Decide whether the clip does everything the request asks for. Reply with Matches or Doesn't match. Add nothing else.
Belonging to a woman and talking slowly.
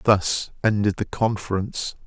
Doesn't match